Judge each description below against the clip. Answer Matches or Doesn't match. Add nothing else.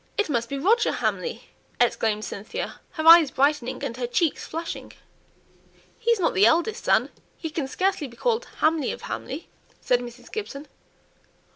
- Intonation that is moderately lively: Doesn't match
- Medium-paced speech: Matches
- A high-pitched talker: Matches